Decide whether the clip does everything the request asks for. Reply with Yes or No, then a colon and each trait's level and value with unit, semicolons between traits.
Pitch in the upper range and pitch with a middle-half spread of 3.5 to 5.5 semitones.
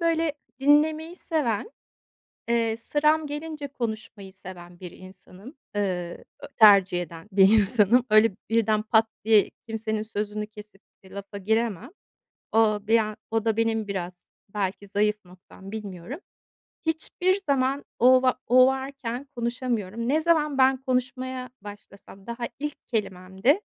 Yes: high, 225 Hz; average, 4.5 semitones